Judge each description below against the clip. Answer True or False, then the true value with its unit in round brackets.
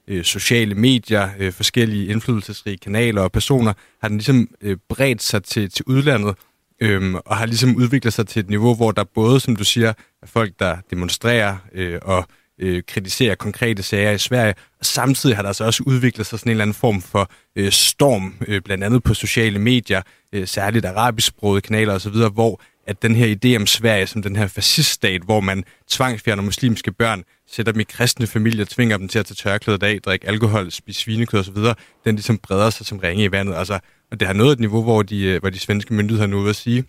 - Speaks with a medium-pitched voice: False (110 Hz)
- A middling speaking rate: True (200 wpm)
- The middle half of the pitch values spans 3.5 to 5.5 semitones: False (2.8 semitones)